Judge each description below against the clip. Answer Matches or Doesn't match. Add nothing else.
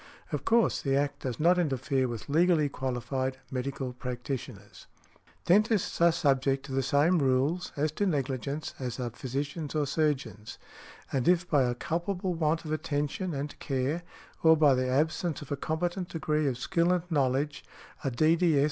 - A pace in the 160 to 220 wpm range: Matches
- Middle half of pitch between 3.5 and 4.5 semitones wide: Matches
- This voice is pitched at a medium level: Matches